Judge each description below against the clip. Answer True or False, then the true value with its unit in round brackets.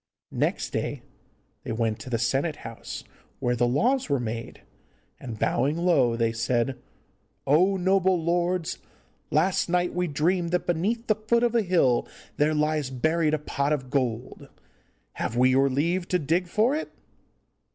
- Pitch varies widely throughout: True (5.9 semitones)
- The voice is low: False (155 Hz)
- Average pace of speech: True (160 wpm)